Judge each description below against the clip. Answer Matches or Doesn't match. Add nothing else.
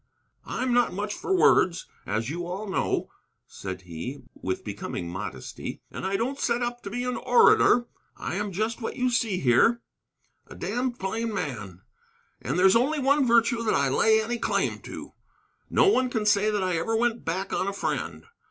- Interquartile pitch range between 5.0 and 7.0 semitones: Matches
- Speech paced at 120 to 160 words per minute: Doesn't match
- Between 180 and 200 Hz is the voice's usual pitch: Doesn't match